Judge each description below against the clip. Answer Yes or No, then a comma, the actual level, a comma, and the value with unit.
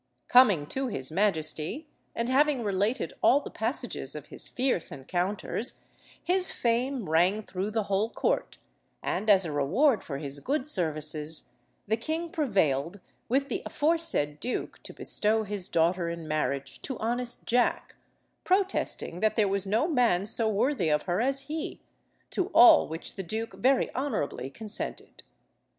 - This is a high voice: Yes, high, 215 Hz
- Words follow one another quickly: No, average, 150 wpm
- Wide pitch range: Yes, wide, 7.4 semitones